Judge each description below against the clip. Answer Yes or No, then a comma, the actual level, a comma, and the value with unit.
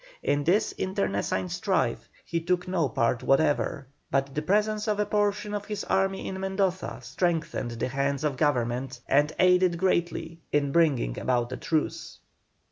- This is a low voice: No, medium, 165 Hz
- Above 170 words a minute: No, average, 155 wpm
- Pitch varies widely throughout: Yes, wide, 5.7 semitones